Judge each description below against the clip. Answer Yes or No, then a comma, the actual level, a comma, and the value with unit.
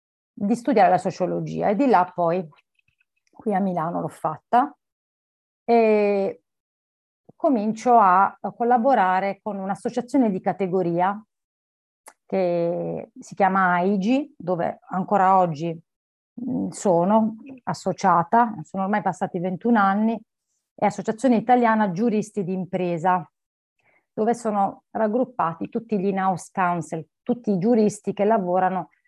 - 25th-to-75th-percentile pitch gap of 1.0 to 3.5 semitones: No, average, 3.9 semitones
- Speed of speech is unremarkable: No, slow, 110 wpm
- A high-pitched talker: Yes, high, 195 Hz